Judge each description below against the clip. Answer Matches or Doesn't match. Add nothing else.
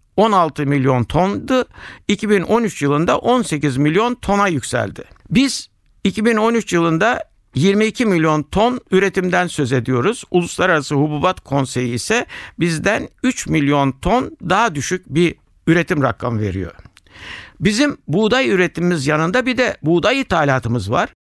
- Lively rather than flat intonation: Matches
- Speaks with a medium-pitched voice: Matches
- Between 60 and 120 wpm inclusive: Matches